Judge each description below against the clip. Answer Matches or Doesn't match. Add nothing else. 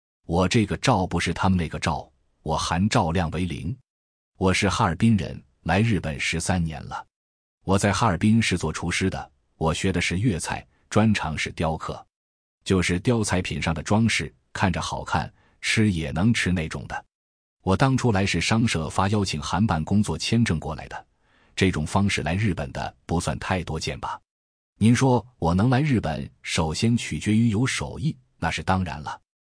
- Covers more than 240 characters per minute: Matches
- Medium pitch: Doesn't match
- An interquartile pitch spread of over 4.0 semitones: Matches